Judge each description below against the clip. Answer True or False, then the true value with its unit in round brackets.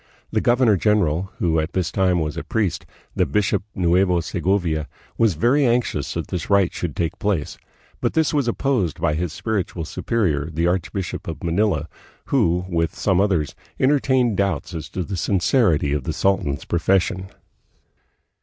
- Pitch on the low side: True (95 Hz)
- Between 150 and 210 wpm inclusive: True (165 wpm)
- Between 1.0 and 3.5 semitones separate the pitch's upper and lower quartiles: False (4.1 semitones)